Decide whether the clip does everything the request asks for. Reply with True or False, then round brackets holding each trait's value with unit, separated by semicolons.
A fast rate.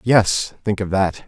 False (140 wpm)